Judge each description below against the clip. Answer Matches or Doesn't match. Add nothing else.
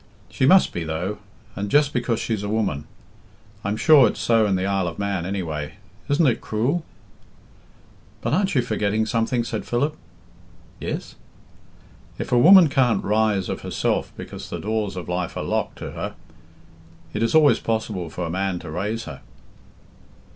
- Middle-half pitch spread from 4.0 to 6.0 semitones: Matches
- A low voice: Matches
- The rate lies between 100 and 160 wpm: Doesn't match